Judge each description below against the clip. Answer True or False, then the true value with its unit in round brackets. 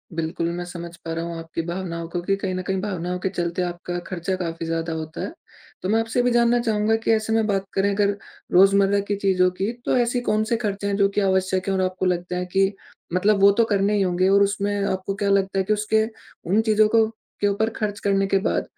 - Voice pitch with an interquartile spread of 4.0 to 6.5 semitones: False (2.5 semitones)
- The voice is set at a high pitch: True (195 Hz)